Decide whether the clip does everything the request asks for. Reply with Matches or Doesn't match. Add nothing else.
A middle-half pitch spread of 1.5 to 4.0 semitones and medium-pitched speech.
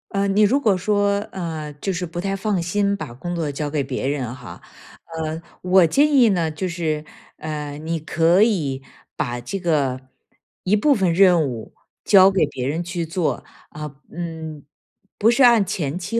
Doesn't match